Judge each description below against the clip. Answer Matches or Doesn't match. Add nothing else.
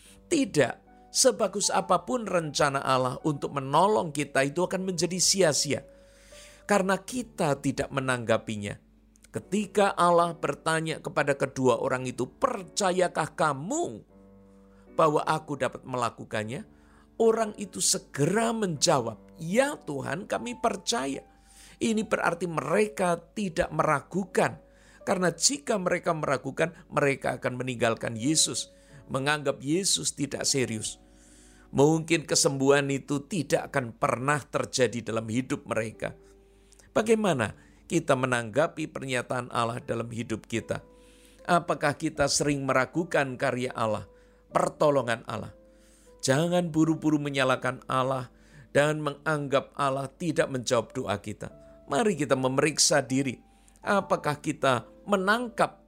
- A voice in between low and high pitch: Matches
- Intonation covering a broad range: Matches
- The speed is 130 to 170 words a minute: Doesn't match